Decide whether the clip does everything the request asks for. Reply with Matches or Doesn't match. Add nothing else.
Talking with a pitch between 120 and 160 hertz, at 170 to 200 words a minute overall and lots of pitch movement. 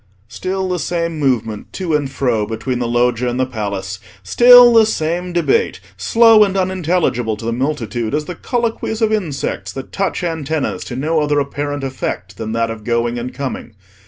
Matches